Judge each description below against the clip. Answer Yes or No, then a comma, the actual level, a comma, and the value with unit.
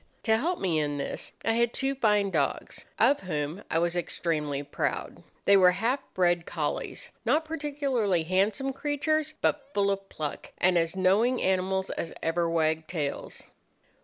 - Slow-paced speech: No, average, 160 wpm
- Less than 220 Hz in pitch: Yes, high, 190 Hz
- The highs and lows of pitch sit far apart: Yes, wide, 7.3 semitones